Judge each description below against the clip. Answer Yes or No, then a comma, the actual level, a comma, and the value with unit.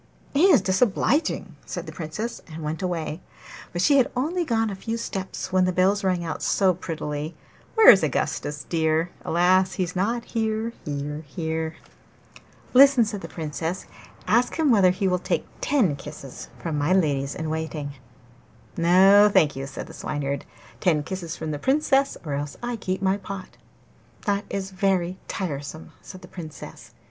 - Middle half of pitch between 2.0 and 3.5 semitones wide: No, average, 4.7 semitones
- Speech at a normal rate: Yes, average, 165 wpm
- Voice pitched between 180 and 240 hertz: Yes, medium, 185 Hz